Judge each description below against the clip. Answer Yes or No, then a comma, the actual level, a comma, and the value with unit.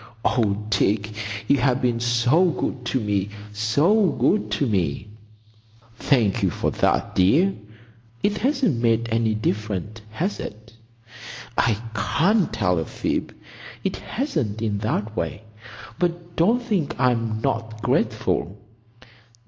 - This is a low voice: Yes, low, 115 Hz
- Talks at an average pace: No, slow, 120 wpm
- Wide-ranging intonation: Yes, wide, 7.1 semitones